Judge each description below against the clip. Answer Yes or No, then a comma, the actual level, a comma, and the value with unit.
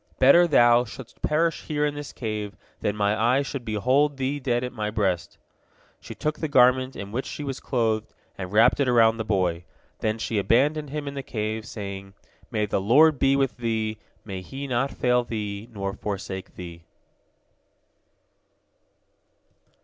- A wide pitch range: No, average, 4.4 semitones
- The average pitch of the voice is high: No, low, 120 Hz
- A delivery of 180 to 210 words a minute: No, average, 165 wpm